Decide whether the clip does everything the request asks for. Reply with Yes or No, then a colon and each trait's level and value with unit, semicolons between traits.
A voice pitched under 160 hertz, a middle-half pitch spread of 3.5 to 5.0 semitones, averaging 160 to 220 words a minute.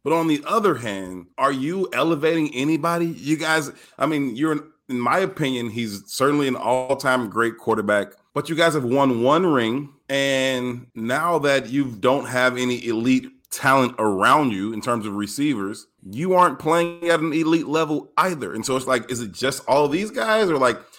Yes: low, 135 Hz; average, 4.7 semitones; average, 190 wpm